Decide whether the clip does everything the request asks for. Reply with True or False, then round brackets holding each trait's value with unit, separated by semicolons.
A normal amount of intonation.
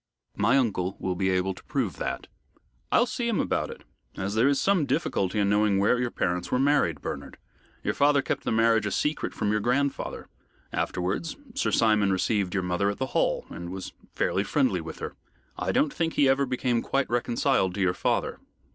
False (6.1 semitones)